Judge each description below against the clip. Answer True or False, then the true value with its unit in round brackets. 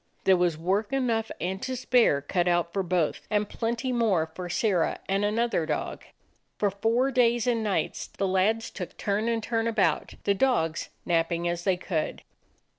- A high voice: True (200 Hz)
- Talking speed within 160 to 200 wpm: True (180 wpm)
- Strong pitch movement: False (4.7 semitones)